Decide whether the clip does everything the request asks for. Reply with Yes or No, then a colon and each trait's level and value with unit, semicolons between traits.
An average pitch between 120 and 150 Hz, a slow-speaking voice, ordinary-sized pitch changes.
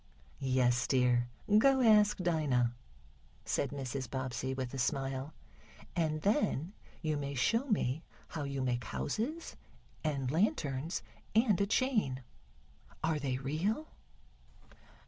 No: medium, 140 Hz; slow, 115 wpm; wide, 7.3 semitones